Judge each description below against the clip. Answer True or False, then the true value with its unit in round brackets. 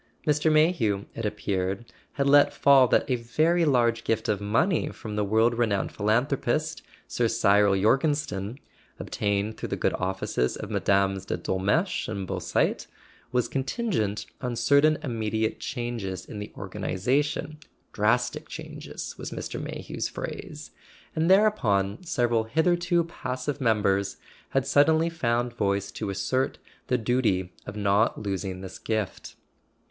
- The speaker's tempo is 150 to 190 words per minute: False (135 wpm)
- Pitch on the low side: True (115 Hz)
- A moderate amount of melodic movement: False (5.9 semitones)